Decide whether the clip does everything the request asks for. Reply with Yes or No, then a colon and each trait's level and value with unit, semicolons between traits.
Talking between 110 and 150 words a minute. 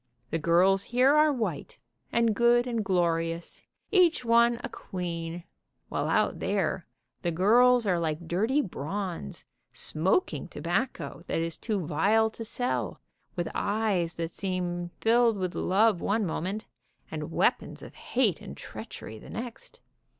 Yes: average, 140 wpm